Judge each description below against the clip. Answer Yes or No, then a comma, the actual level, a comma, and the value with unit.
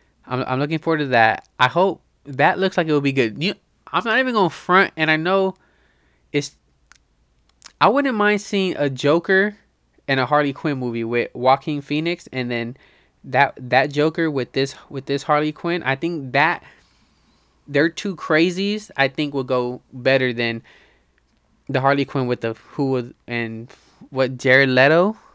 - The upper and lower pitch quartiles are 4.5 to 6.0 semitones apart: Yes, average, 5.0 semitones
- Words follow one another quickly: No, average, 170 wpm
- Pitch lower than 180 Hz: Yes, medium, 140 Hz